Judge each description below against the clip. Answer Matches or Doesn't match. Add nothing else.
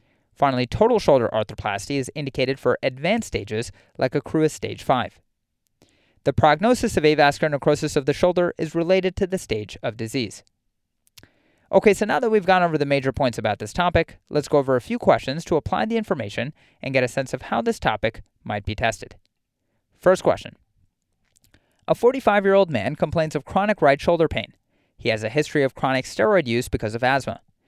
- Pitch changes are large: Matches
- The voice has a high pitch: Doesn't match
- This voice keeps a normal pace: Matches